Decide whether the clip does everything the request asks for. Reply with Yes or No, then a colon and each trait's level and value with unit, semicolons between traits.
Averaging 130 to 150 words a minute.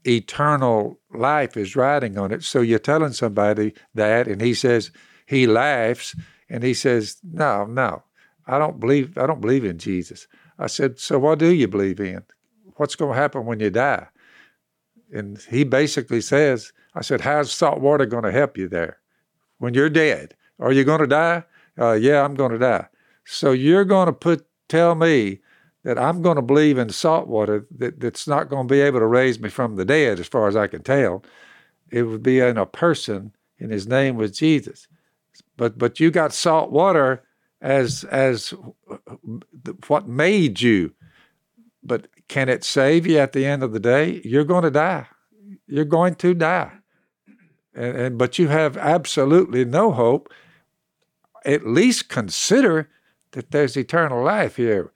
No: average, 180 wpm